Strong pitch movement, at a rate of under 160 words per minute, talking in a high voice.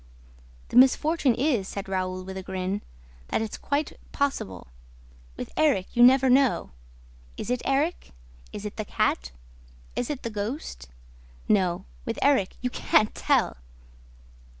Yes: wide, 6.1 semitones; average, 140 wpm; high, 225 Hz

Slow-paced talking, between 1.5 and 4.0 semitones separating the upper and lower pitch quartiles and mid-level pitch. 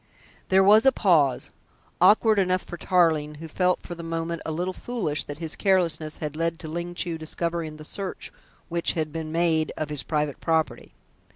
No: average, 185 wpm; narrow, 2.6 semitones; medium, 165 Hz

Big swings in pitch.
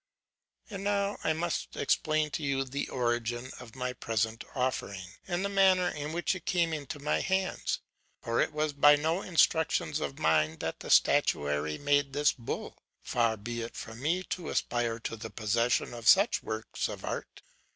Yes: wide, 5.8 semitones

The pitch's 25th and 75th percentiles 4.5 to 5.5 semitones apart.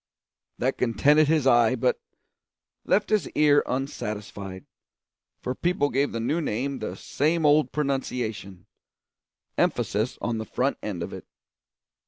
Yes: average, 5.1 semitones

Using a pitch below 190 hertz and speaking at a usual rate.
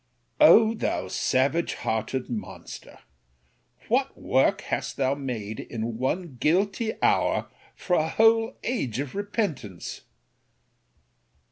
No: medium, 140 Hz; slow, 105 wpm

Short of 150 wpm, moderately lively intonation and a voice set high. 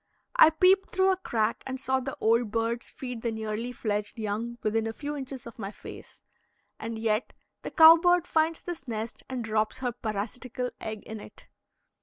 No: average, 185 wpm; average, 3.9 semitones; high, 235 Hz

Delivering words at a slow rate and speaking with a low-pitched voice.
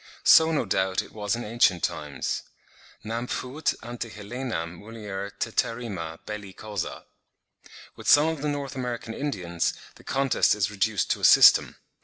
No: average, 150 wpm; low, 110 Hz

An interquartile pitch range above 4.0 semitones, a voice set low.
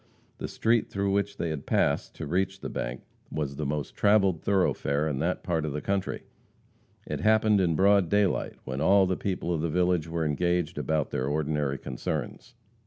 Yes: average, 4.7 semitones; very low, 85 Hz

